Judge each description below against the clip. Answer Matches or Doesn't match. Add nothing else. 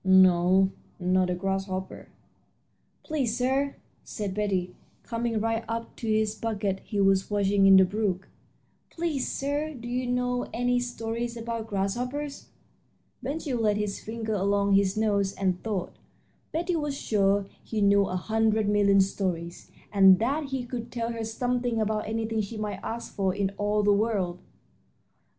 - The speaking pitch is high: Matches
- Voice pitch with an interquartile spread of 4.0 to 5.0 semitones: Doesn't match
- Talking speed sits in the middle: Matches